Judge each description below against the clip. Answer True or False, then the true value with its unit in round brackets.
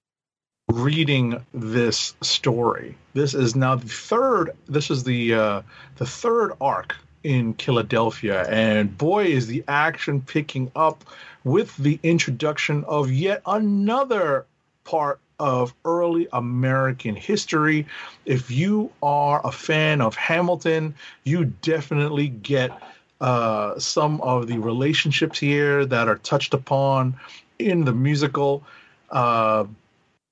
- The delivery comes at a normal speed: False (115 wpm)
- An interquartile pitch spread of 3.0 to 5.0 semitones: True (3.9 semitones)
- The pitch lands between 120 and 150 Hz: True (140 Hz)